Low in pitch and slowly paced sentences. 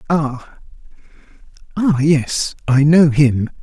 No: medium, 145 Hz; slow, 85 wpm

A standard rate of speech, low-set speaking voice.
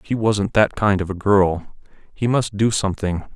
Yes: average, 195 wpm; low, 100 Hz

